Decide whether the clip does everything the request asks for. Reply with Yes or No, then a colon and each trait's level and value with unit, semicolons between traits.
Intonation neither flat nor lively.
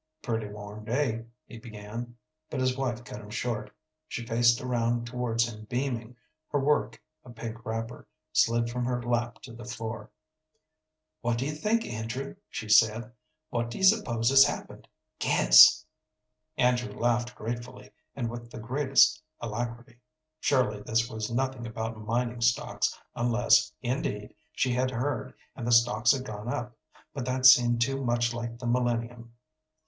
No: narrow, 1.6 semitones